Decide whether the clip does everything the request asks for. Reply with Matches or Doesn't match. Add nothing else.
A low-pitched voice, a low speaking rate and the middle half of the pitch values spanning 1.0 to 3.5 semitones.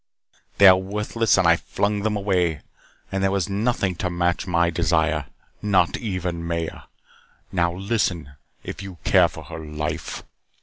Doesn't match